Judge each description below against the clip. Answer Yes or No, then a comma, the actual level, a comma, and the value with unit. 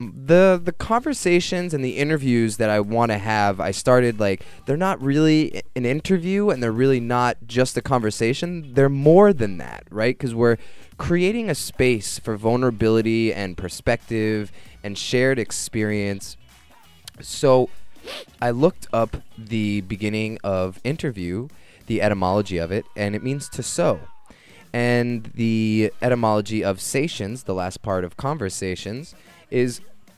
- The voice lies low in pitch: Yes, low, 115 Hz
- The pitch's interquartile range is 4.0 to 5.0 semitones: Yes, average, 4.5 semitones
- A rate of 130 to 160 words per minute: Yes, average, 140 wpm